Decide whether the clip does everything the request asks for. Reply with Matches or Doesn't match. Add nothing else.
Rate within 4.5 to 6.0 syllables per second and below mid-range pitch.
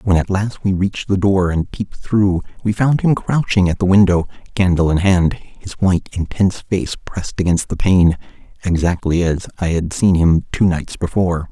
Matches